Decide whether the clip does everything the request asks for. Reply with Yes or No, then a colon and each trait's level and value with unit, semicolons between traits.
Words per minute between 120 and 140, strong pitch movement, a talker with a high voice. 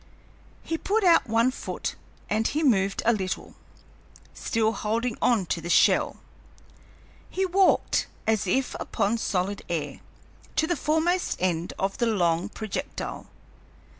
Yes: slow, 135 wpm; wide, 6.8 semitones; high, 220 Hz